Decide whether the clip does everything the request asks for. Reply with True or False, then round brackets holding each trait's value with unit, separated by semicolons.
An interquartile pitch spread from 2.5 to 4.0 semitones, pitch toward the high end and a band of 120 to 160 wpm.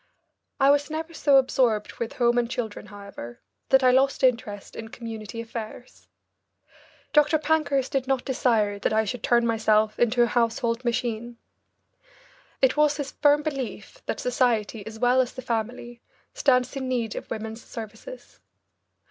True (3.1 semitones; 240 Hz; 155 wpm)